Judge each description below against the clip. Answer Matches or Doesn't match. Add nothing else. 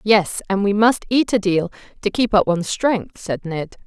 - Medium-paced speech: Doesn't match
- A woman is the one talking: Matches